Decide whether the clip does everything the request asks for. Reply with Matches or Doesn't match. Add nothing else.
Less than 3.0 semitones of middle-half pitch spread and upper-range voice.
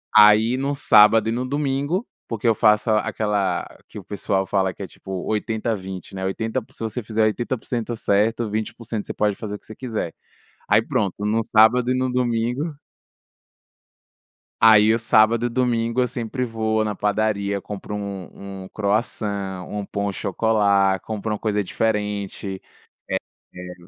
Doesn't match